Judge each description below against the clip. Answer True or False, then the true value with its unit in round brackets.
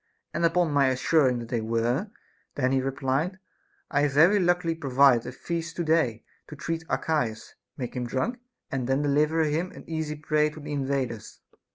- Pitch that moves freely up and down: False (3.8 semitones)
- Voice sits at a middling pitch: True (145 Hz)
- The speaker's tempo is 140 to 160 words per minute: False (180 wpm)